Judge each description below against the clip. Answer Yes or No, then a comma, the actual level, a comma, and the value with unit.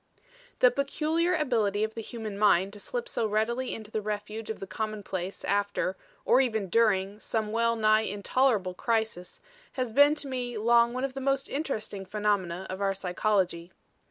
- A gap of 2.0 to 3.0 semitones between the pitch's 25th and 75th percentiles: No, average, 3.5 semitones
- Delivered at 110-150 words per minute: No, average, 170 wpm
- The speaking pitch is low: No, high, 220 Hz